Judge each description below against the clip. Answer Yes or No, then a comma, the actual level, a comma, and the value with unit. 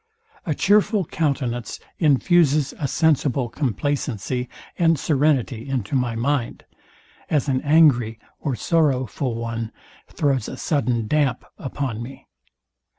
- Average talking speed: No, slow, 110 wpm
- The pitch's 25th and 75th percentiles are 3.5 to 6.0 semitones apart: Yes, average, 3.9 semitones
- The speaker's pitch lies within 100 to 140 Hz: Yes, low, 135 Hz